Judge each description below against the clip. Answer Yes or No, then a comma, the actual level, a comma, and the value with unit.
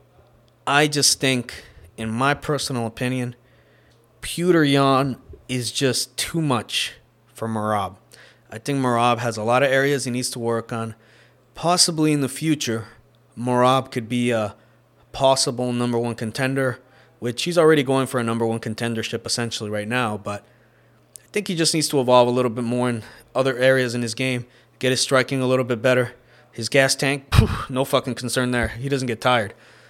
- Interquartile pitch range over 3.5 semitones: No, narrow, 2.5 semitones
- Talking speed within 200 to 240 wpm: No, average, 175 wpm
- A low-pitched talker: Yes, low, 125 Hz